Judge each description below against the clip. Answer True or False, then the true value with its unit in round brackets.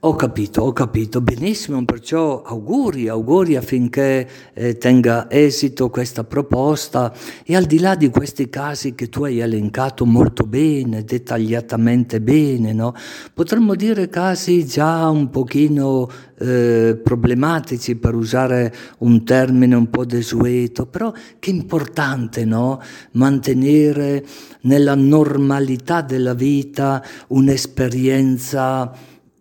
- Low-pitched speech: True (130 Hz)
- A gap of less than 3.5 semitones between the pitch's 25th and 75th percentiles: True (3.0 semitones)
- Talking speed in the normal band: False (110 wpm)